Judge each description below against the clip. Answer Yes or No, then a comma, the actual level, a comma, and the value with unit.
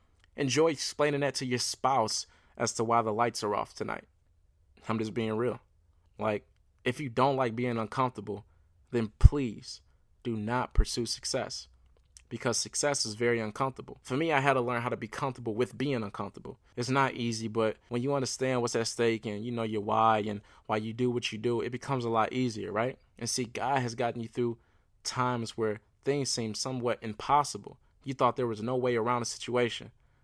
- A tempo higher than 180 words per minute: Yes, average, 195 wpm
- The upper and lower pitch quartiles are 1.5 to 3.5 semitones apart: Yes, average, 2.9 semitones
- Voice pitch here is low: Yes, low, 115 Hz